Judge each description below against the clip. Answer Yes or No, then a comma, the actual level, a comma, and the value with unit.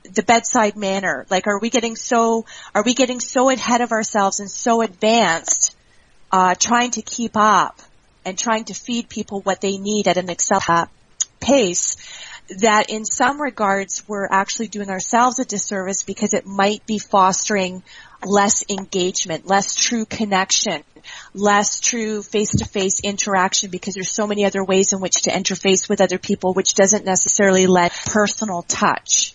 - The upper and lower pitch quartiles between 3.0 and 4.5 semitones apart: No, narrow, 2.6 semitones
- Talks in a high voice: Yes, high, 200 Hz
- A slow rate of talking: No, average, 165 wpm